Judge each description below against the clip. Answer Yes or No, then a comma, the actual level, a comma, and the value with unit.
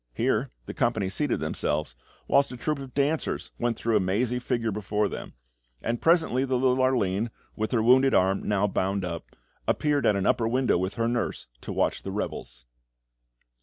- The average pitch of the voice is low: Yes, low, 115 Hz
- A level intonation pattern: No, average, 4.8 semitones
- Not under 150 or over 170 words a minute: No, average, 180 wpm